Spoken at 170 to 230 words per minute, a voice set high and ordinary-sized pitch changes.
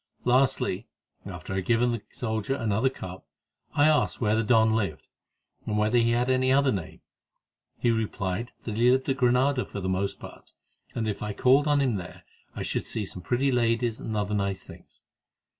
No: average, 195 wpm; low, 115 Hz; average, 3.8 semitones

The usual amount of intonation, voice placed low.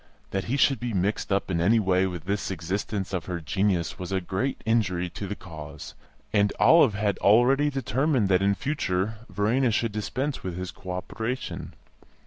Yes: average, 4.0 semitones; low, 100 Hz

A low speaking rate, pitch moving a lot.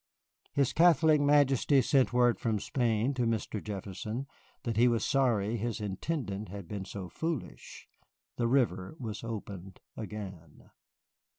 No: slow, 130 wpm; average, 4.7 semitones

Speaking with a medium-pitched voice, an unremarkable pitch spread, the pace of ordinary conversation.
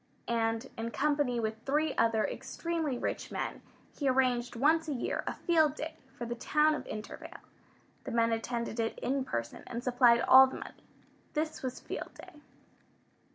No: very high, 255 Hz; average, 4.5 semitones; average, 165 wpm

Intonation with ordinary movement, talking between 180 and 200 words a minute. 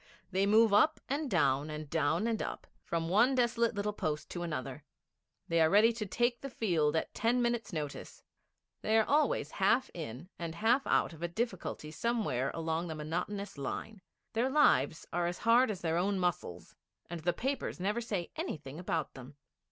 No: wide, 6.2 semitones; average, 185 wpm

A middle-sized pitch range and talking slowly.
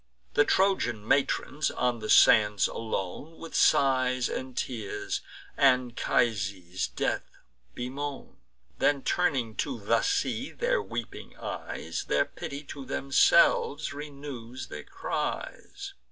Yes: average, 4.0 semitones; slow, 110 wpm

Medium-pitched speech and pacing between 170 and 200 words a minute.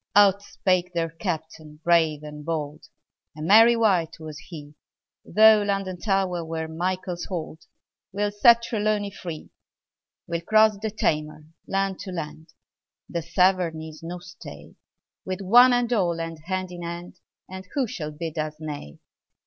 No: medium, 175 Hz; average, 150 wpm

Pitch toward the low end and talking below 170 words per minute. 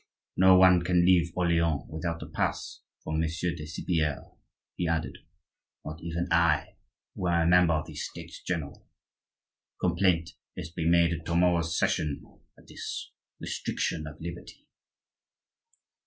Yes: very low, 85 Hz; average, 140 wpm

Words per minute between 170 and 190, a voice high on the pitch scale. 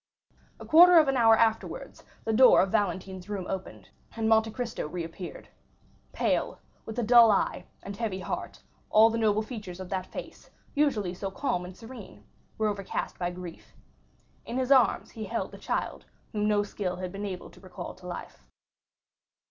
Yes: average, 175 wpm; high, 210 Hz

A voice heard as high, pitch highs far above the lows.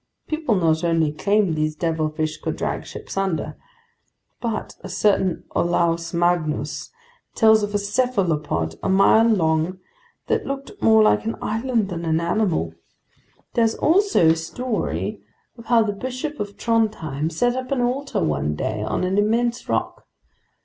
Yes: high, 195 Hz; wide, 6.1 semitones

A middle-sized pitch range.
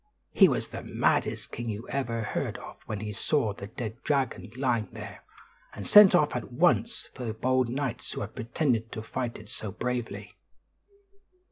Yes: average, 3.1 semitones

